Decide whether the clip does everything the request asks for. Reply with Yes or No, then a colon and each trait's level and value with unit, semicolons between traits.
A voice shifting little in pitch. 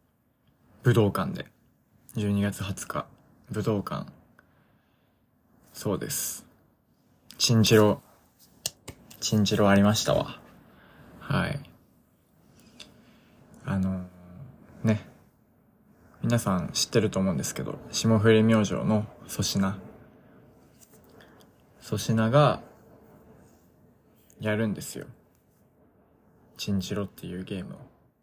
Yes: narrow, 2.1 semitones